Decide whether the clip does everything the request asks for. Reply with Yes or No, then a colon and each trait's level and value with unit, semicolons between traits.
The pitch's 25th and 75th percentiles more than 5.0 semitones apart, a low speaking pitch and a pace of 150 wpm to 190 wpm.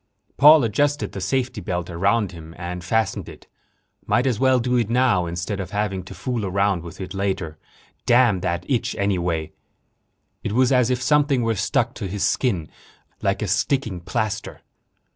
Yes: wide, 5.5 semitones; low, 105 Hz; average, 170 wpm